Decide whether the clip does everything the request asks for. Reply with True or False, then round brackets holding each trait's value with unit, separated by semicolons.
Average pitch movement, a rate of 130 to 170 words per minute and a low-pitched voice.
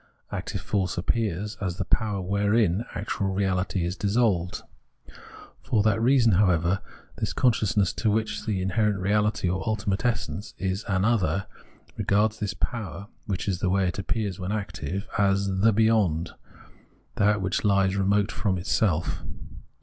False (2.3 semitones; 155 wpm; 100 Hz)